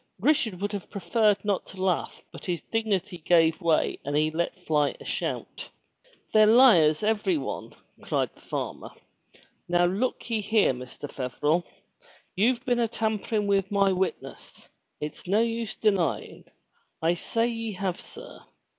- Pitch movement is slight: No, average, 4.4 semitones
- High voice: Yes, high, 195 Hz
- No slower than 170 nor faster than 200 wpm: No, average, 150 wpm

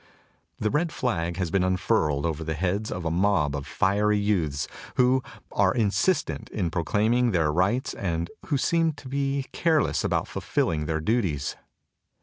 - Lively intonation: Yes, wide, 7.0 semitones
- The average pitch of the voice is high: No, very low, 95 Hz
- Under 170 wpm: Yes, average, 160 wpm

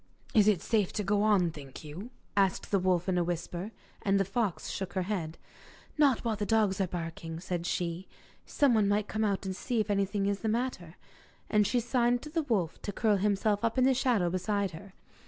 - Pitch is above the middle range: Yes, high, 200 Hz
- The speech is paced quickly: Yes, fast, 210 wpm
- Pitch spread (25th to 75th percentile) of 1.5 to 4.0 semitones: Yes, average, 3.4 semitones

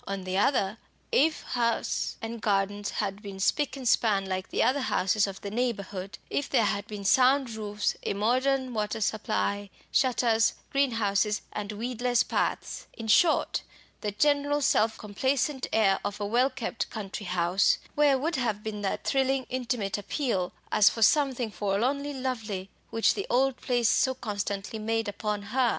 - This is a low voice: No, high, 220 Hz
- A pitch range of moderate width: Yes, average, 4.2 semitones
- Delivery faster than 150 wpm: Yes, average, 160 wpm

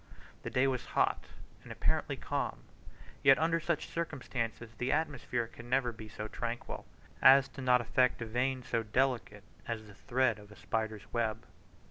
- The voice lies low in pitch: Yes, low, 120 Hz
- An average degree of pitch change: Yes, average, 3.0 semitones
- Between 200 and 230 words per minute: No, average, 165 wpm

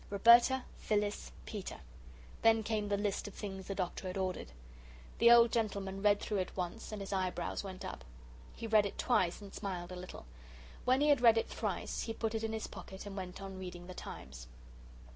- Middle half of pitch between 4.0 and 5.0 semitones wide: No, average, 3.1 semitones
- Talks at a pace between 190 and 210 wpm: Yes, average, 200 wpm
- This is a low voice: No, high, 200 Hz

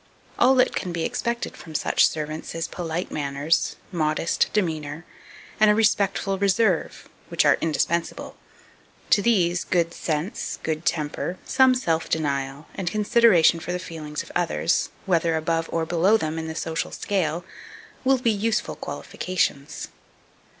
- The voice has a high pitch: No, medium, 170 Hz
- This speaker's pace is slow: No, average, 145 wpm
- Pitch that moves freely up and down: No, average, 4.0 semitones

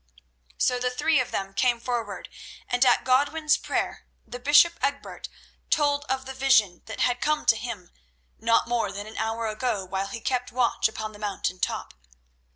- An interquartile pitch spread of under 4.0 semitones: Yes, average, 3.4 semitones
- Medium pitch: No, high, 245 Hz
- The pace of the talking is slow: No, average, 175 wpm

